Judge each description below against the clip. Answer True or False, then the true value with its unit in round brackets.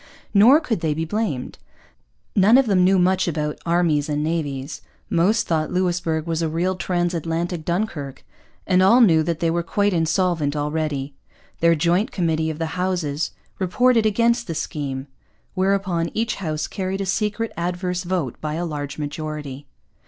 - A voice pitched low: False (170 Hz)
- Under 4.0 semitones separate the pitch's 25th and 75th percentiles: True (3.4 semitones)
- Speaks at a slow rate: False (160 wpm)